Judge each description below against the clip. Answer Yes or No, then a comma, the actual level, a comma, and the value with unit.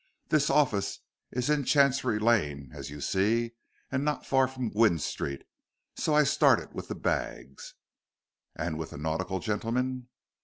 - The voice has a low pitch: Yes, low, 115 Hz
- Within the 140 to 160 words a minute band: Yes, average, 150 wpm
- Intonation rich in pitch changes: Yes, wide, 7.2 semitones